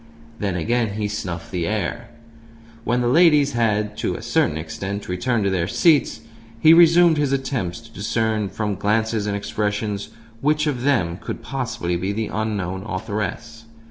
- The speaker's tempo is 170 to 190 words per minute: No, average, 160 wpm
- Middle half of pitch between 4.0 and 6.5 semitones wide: No, average, 3.6 semitones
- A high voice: No, low, 110 Hz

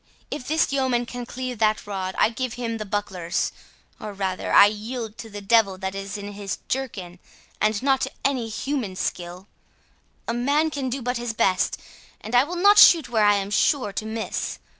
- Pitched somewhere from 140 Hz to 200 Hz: No, high, 225 Hz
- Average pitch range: Yes, average, 4.2 semitones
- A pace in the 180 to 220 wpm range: Yes, average, 190 wpm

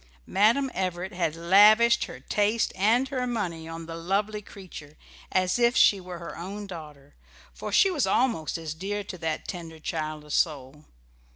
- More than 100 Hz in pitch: Yes, medium, 185 Hz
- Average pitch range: Yes, average, 4.5 semitones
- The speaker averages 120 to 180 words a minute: Yes, average, 165 wpm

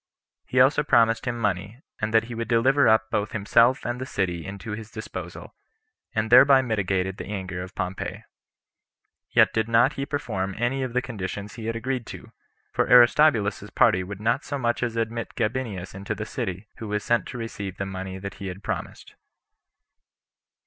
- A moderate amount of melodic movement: Yes, average, 3.5 semitones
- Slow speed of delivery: No, average, 185 wpm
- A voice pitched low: Yes, low, 110 Hz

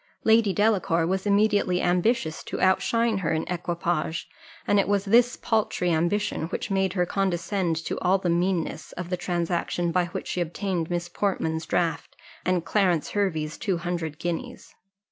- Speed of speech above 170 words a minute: No, average, 160 wpm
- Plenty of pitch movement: No, average, 2.7 semitones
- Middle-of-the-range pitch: Yes, medium, 180 Hz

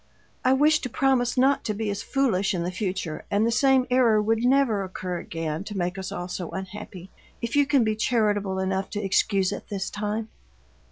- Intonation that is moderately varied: Yes, average, 4.5 semitones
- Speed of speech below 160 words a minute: No, fast, 205 wpm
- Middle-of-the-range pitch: No, high, 210 Hz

